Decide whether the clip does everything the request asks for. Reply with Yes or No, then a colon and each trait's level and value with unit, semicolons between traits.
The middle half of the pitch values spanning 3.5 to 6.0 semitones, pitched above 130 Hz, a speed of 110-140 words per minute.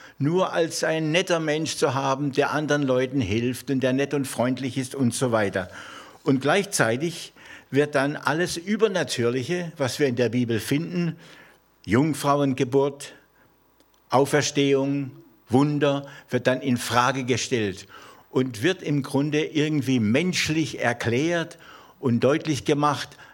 No: average, 3.0 semitones; medium, 140 Hz; average, 130 wpm